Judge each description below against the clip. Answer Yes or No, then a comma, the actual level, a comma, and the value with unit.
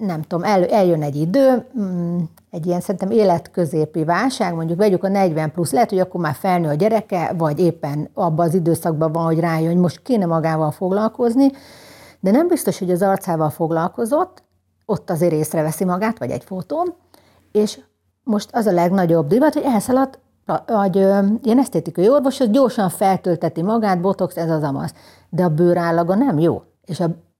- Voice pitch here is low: No, medium, 185 Hz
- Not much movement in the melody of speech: No, average, 4.4 semitones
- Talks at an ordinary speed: No, fast, 170 wpm